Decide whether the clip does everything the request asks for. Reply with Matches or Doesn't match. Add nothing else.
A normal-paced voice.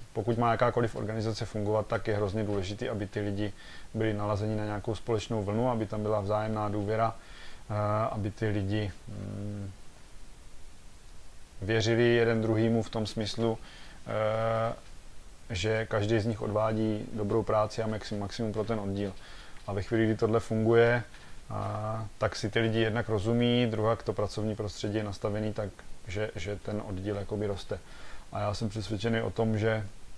Matches